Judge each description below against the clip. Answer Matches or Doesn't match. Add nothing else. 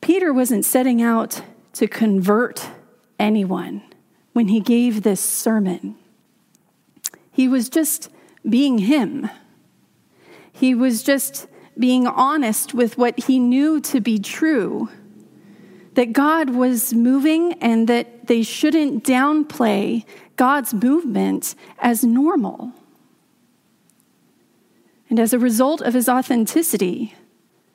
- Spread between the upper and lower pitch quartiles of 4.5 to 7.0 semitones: Doesn't match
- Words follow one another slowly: Matches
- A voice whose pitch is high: Matches